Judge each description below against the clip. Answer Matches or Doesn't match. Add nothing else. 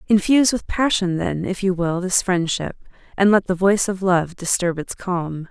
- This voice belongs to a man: Doesn't match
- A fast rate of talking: Doesn't match